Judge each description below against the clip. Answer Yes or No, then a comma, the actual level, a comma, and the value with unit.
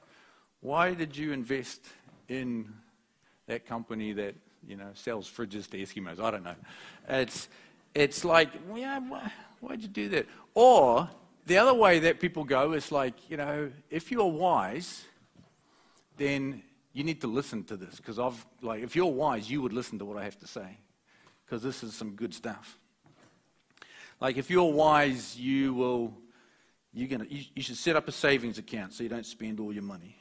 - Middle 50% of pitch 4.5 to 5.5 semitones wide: Yes, average, 5.1 semitones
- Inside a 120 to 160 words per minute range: No, average, 180 wpm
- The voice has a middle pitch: No, low, 130 Hz